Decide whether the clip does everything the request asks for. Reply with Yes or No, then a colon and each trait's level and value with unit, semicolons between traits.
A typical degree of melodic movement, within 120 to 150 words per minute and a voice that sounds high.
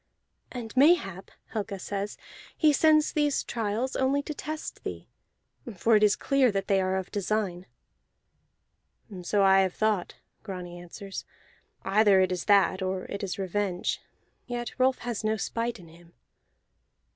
Yes: average, 4.2 semitones; average, 145 wpm; high, 205 Hz